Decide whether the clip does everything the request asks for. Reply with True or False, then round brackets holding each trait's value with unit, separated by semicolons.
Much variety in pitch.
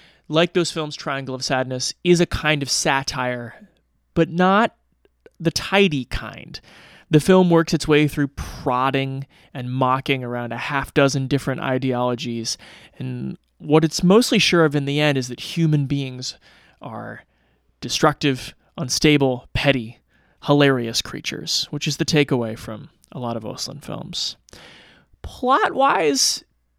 False (4.1 semitones)